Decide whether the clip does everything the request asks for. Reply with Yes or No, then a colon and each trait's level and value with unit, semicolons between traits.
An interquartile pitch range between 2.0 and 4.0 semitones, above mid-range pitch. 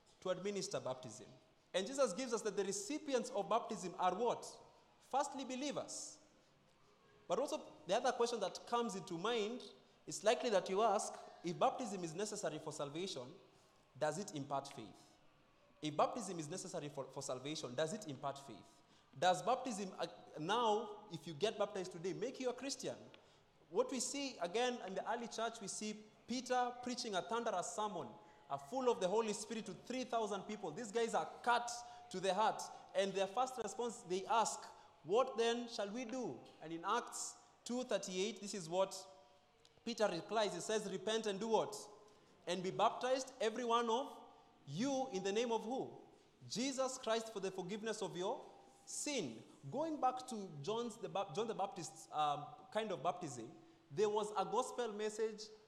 No: average, 4.7 semitones; high, 215 Hz